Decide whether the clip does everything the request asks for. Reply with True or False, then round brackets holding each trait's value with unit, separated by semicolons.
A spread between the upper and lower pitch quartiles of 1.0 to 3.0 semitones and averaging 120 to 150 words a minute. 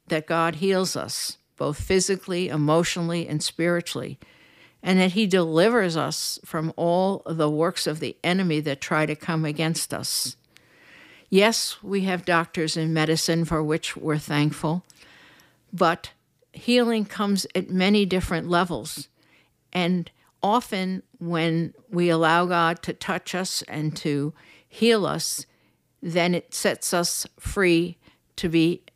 True (2.7 semitones; 135 wpm)